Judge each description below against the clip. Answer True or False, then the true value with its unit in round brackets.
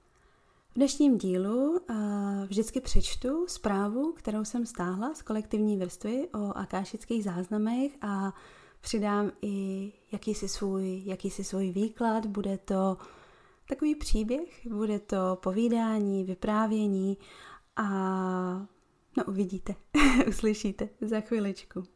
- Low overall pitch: False (210 Hz)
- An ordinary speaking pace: False (105 wpm)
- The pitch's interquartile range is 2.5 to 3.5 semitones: True (2.9 semitones)